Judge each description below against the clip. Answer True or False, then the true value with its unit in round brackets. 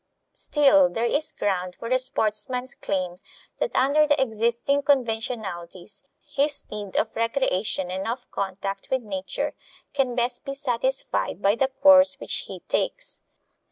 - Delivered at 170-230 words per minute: False (140 wpm)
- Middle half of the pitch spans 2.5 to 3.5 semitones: False (5.4 semitones)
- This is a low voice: False (235 Hz)